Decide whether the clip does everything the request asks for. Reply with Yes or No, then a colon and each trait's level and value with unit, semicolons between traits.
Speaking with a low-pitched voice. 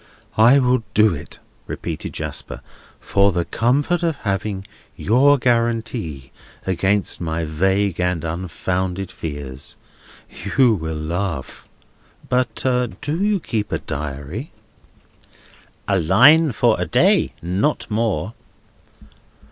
Yes: low, 100 Hz